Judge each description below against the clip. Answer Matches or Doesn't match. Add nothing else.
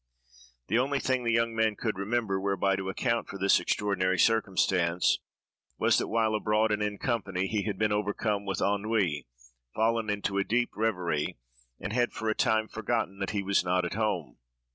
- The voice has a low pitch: Matches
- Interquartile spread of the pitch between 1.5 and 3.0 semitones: Matches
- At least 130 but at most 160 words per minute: Doesn't match